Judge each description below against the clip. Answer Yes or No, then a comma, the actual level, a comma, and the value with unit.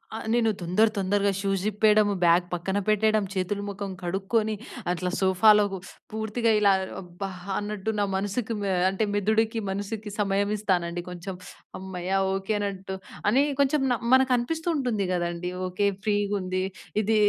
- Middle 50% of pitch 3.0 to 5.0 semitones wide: No, narrow, 2.4 semitones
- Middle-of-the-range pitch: No, high, 205 Hz